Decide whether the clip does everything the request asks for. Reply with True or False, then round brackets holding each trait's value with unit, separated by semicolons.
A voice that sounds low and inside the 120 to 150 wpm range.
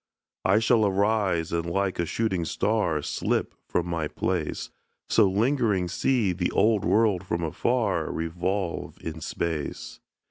True (95 Hz; 135 wpm)